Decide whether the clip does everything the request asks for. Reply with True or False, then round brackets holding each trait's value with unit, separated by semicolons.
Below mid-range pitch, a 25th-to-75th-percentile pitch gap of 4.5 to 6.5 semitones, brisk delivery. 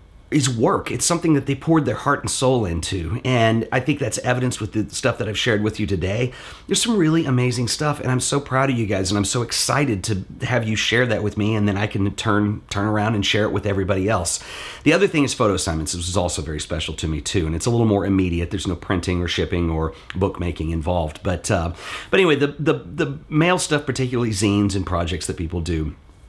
True (105 Hz; 5.5 semitones; 240 wpm)